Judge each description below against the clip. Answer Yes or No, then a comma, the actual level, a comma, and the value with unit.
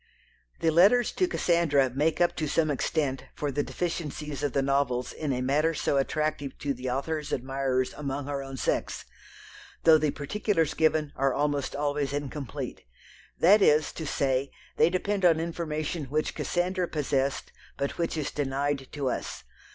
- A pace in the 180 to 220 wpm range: No, average, 160 wpm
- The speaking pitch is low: No, medium, 145 Hz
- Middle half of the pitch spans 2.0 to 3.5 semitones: Yes, average, 2.9 semitones